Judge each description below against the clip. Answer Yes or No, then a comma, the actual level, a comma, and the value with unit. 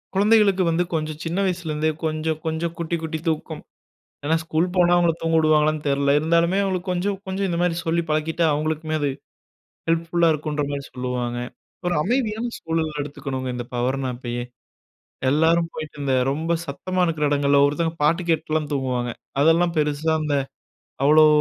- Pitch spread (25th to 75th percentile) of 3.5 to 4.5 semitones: No, narrow, 2.6 semitones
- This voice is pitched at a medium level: Yes, medium, 155 Hz